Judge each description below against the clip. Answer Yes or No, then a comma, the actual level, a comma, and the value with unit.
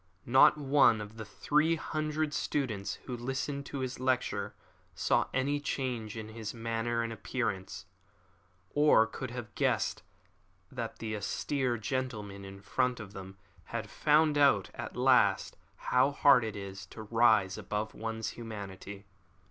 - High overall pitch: No, low, 115 Hz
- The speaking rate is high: No, average, 140 wpm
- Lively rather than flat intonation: No, average, 4.0 semitones